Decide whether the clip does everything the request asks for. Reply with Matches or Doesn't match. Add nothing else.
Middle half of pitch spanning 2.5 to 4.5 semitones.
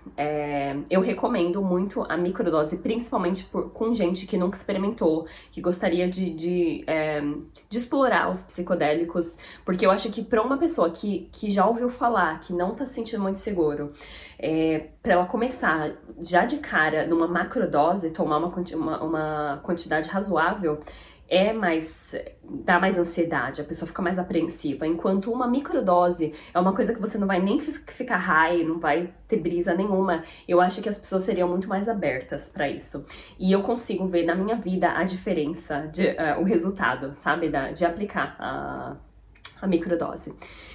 Matches